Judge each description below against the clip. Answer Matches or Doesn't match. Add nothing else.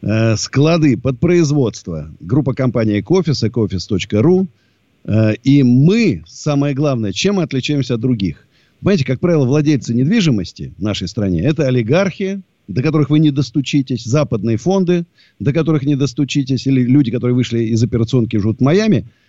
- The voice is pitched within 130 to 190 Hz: Matches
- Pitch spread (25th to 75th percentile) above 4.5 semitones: Matches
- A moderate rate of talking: Matches